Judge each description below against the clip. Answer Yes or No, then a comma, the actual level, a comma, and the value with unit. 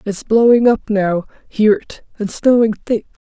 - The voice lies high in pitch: Yes, high, 220 Hz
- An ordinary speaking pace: Yes, average, 165 wpm